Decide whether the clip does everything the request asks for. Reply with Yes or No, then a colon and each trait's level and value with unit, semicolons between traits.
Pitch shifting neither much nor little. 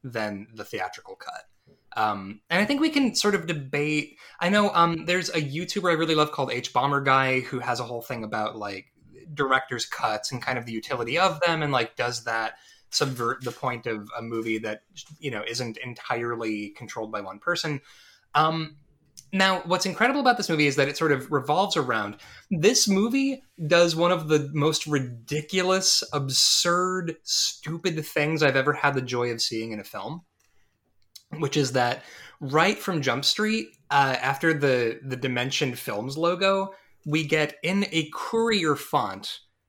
No: wide, 5.9 semitones